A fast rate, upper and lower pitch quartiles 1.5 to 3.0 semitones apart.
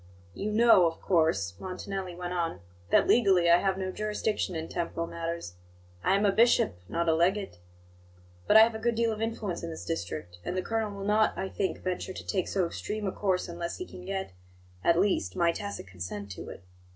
No: fast, 210 wpm; average, 3.7 semitones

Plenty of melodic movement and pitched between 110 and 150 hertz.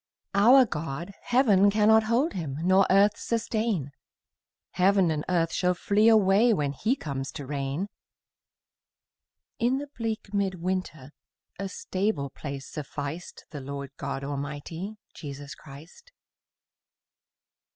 No: wide, 6.9 semitones; medium, 185 Hz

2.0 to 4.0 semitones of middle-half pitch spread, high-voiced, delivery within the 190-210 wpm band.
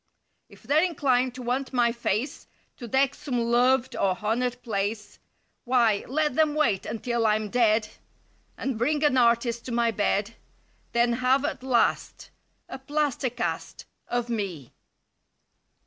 No: narrow, 2.6 semitones; high, 240 Hz; average, 140 wpm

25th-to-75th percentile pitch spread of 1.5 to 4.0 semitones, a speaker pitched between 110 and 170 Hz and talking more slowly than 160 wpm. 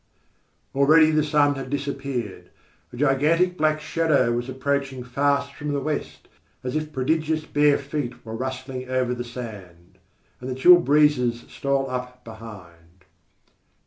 Yes: average, 3.3 semitones; low, 135 Hz; average, 140 wpm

